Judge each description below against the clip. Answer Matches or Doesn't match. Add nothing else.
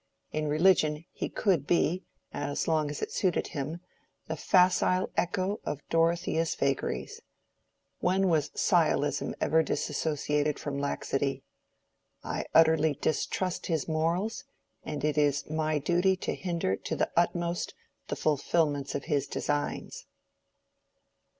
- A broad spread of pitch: Doesn't match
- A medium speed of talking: Doesn't match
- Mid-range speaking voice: Matches